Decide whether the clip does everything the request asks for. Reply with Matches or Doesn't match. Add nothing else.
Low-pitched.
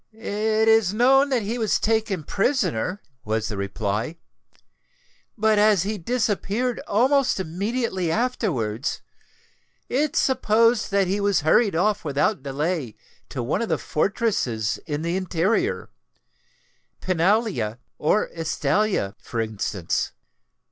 Doesn't match